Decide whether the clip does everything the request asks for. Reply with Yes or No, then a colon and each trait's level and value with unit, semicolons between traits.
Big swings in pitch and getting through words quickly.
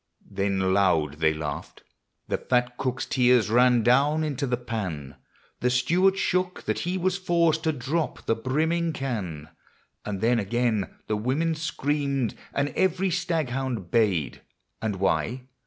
No: wide, 6.9 semitones; average, 145 wpm